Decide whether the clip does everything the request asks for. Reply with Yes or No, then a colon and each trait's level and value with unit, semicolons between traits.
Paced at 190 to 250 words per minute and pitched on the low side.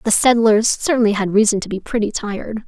No: average, 200 wpm; high, 215 Hz